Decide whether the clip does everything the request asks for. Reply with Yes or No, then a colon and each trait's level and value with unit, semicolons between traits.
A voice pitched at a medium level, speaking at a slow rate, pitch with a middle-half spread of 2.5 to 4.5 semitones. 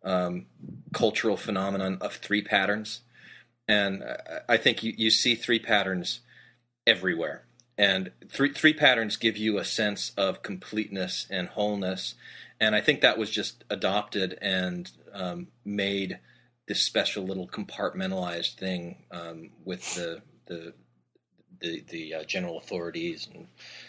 No: low, 100 Hz; slow, 130 wpm; average, 3.6 semitones